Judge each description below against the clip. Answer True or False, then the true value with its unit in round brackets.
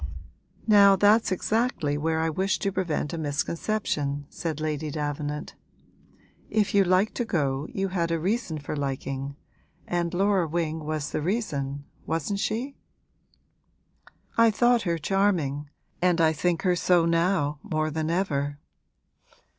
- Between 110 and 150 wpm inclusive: True (140 wpm)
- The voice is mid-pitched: True (165 Hz)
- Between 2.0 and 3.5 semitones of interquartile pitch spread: False (4.7 semitones)